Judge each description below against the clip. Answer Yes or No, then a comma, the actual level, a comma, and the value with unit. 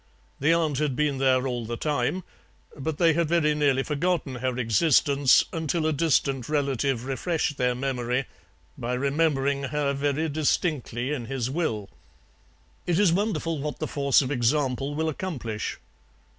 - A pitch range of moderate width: Yes, average, 3.3 semitones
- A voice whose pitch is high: No, medium, 140 Hz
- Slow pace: No, average, 150 wpm